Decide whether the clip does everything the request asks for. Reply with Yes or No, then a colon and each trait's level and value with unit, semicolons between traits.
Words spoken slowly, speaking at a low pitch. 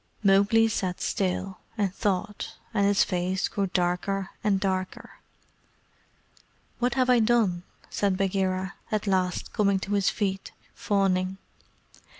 No: slow, 125 wpm; high, 195 Hz